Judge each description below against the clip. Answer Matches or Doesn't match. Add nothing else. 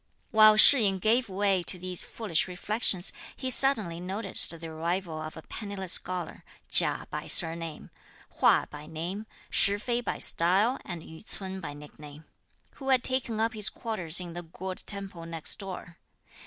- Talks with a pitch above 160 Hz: Matches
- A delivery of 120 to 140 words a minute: Doesn't match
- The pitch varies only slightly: Doesn't match